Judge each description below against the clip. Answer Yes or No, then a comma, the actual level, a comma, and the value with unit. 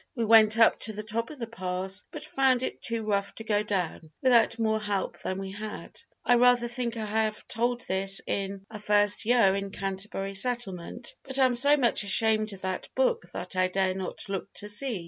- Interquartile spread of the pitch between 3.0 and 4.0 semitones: Yes, average, 3.4 semitones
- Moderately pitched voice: No, high, 215 Hz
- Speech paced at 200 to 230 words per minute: Yes, fast, 205 wpm